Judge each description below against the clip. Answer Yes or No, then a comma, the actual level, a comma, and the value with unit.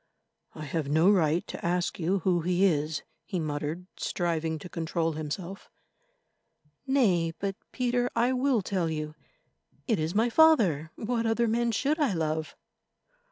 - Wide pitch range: Yes, wide, 6.0 semitones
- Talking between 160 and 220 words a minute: No, average, 145 wpm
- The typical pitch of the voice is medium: Yes, medium, 180 Hz